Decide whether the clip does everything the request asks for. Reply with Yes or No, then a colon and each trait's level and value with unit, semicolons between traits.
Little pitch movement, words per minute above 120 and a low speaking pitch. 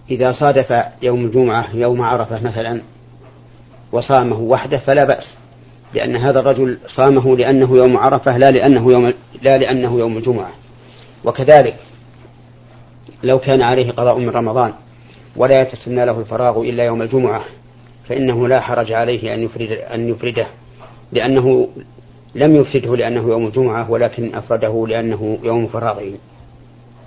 Yes: narrow, 1.7 semitones; average, 130 wpm; low, 120 Hz